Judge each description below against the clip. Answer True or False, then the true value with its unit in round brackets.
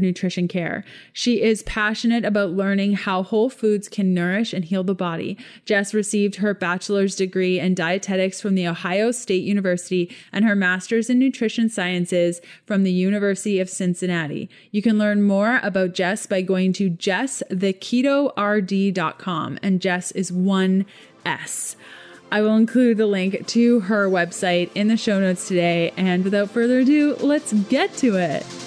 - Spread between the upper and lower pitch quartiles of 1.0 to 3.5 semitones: True (2.8 semitones)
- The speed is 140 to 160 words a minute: True (155 wpm)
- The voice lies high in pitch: True (195 Hz)